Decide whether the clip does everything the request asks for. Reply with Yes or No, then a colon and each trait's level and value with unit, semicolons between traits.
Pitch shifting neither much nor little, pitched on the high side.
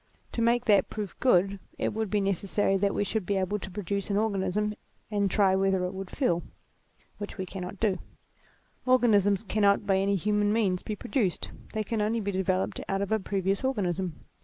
No: narrow, 1.8 semitones; high, 200 Hz